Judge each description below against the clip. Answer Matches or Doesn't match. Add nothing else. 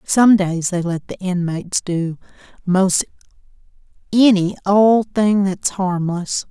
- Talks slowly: Matches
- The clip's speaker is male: Doesn't match